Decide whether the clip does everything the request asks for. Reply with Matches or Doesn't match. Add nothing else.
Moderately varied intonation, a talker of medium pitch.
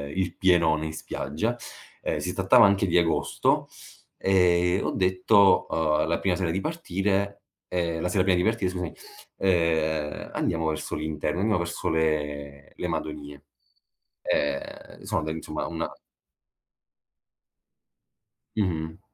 Doesn't match